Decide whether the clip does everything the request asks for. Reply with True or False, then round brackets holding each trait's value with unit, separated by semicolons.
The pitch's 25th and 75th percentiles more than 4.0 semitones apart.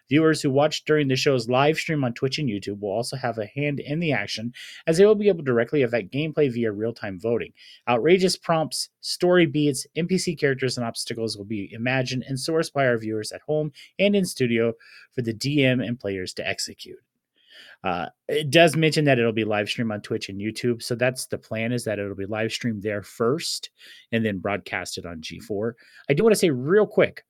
True (5.4 semitones)